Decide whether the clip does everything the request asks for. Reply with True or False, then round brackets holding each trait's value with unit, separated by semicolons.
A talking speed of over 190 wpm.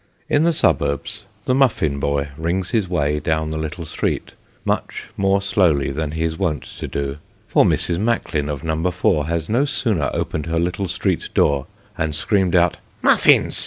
False (180 wpm)